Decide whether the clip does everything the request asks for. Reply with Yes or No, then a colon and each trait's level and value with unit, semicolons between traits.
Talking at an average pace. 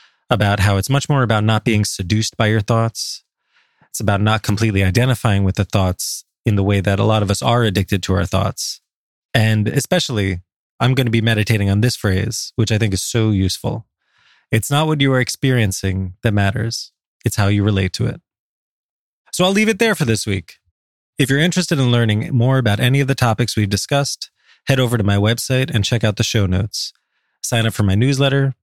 No: fast, 210 wpm